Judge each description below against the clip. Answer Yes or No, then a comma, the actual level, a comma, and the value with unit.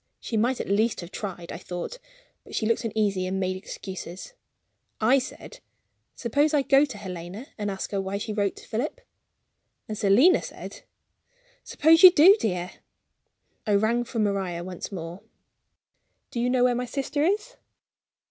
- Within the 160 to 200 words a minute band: Yes, average, 165 wpm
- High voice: Yes, high, 215 Hz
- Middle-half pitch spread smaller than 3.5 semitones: No, wide, 5.4 semitones